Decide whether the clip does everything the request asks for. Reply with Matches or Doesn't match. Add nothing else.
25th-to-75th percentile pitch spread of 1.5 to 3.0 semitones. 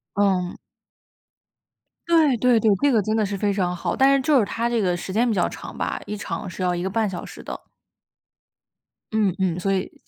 Doesn't match